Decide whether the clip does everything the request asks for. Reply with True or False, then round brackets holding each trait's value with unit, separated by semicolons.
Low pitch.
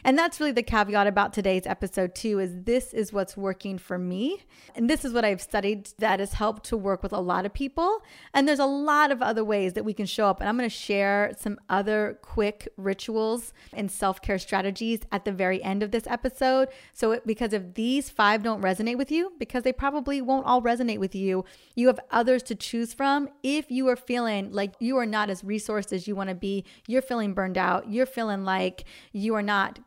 False (215 Hz)